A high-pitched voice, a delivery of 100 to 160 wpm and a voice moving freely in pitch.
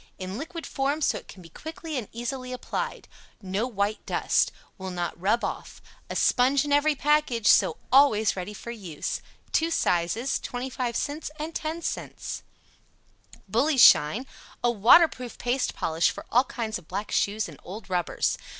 Yes: high, 240 Hz; average, 155 wpm; wide, 6.2 semitones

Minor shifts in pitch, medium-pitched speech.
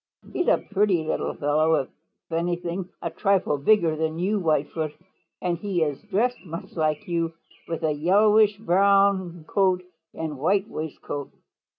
No: average, 4.0 semitones; medium, 175 Hz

